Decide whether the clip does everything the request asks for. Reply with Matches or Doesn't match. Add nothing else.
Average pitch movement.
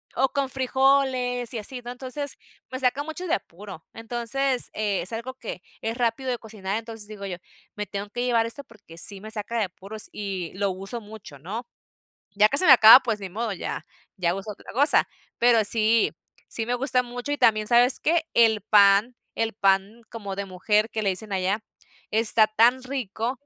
Matches